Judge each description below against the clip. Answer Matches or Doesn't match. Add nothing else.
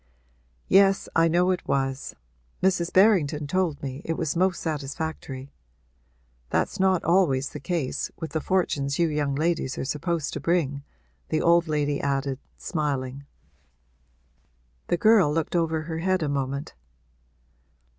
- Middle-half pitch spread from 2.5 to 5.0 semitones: Matches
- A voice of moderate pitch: Matches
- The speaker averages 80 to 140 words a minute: Matches